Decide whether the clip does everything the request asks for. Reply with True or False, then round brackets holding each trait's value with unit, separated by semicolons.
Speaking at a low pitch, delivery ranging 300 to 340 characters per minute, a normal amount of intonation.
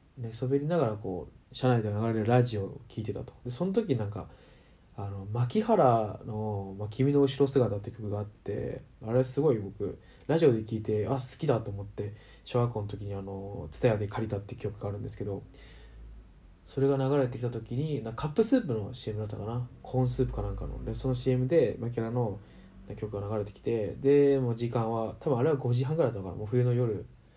False (115 Hz; 390 characters per minute; 3.9 semitones)